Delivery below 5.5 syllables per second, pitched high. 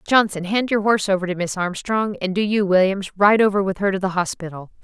No: 5.9 syllables/s; high, 195 Hz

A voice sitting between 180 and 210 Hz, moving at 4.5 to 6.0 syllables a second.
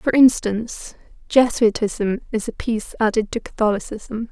No: high, 225 Hz; 4.7 syllables/s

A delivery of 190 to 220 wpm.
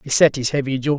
No: fast, 305 wpm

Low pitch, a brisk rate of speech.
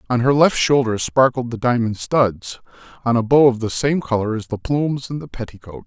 Yes: low, 120 Hz; fast, 215 wpm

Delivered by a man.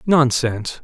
Yes: male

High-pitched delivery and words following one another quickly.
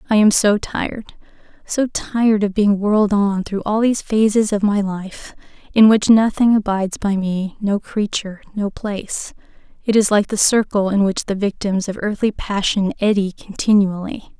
No: high, 205 Hz; average, 165 wpm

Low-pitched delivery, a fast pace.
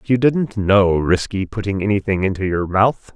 No: low, 100 Hz; average, 190 wpm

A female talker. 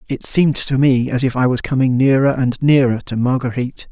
No: male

